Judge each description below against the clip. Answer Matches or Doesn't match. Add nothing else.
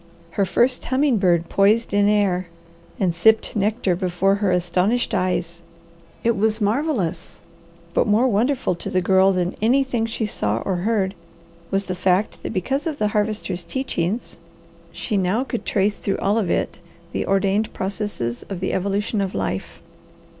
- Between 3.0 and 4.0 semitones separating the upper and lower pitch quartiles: Matches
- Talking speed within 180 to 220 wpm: Doesn't match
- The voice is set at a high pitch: Matches